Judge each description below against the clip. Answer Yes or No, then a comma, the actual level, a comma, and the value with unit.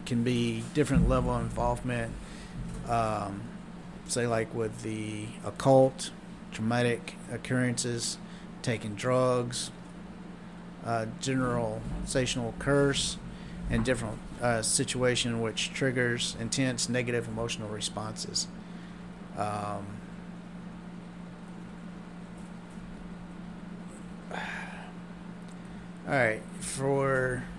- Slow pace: Yes, slow, 75 wpm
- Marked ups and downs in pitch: Yes, wide, 7.4 semitones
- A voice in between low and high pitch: Yes, medium, 150 Hz